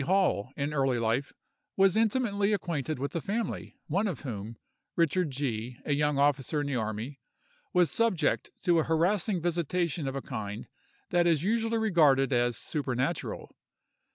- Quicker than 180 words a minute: No, average, 155 wpm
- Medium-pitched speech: Yes, medium, 150 Hz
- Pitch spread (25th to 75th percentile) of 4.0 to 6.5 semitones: Yes, wide, 5.5 semitones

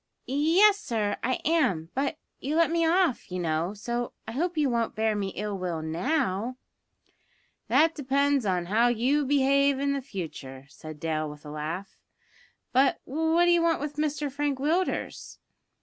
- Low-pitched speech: No, very high, 260 Hz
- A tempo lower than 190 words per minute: Yes, average, 155 wpm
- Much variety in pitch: Yes, wide, 7.6 semitones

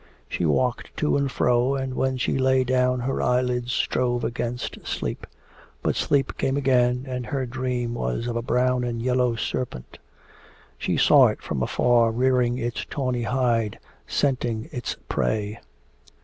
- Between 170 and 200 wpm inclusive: No, average, 150 wpm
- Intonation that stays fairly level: Yes, narrow, 1.4 semitones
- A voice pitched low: Yes, low, 125 Hz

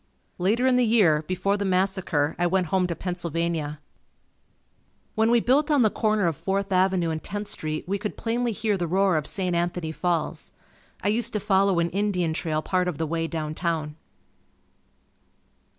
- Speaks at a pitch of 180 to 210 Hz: Yes, medium, 185 Hz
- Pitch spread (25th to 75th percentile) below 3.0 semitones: No, average, 3.6 semitones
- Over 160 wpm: Yes, average, 180 wpm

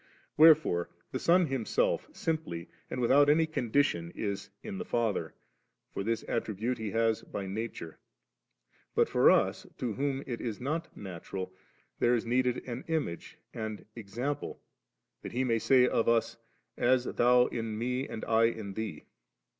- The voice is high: No, low, 120 Hz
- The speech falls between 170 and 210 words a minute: No, average, 155 wpm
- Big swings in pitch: No, average, 3.6 semitones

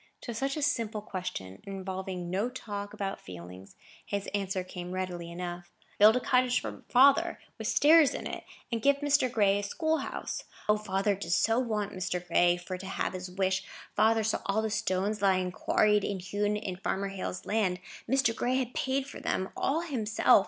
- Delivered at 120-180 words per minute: No, average, 190 wpm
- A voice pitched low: No, high, 200 Hz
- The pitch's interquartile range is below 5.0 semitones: Yes, average, 3.7 semitones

